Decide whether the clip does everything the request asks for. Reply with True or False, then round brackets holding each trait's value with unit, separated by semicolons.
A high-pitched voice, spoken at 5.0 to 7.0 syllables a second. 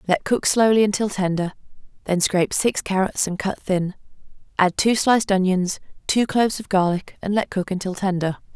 True (195 Hz; 5.3 syllables/s)